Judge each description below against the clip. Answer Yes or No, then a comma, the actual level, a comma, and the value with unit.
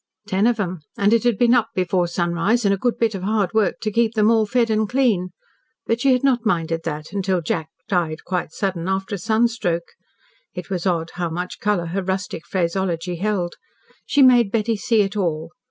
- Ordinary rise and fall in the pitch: Yes, average, 4.2 semitones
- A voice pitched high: Yes, high, 195 Hz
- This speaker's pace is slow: No, fast, 205 wpm